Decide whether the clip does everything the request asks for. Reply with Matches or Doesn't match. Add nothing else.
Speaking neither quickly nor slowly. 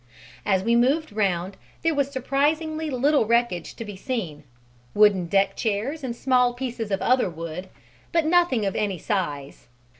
Matches